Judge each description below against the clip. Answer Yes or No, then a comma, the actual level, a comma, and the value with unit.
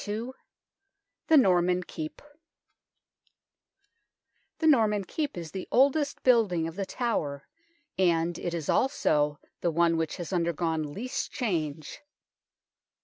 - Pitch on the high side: No, medium, 180 Hz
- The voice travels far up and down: Yes, wide, 6.1 semitones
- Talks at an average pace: No, slow, 115 wpm